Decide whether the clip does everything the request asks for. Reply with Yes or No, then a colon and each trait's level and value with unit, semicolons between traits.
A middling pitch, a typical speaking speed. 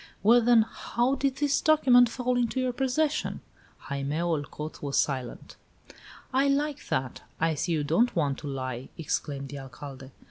Yes: medium, 170 Hz; average, 155 wpm